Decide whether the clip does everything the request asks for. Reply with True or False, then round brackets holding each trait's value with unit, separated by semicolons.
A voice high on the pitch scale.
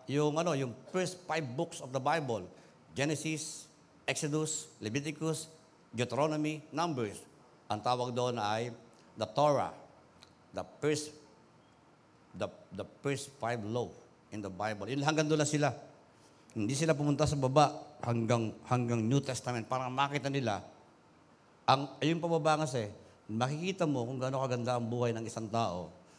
False (140 Hz)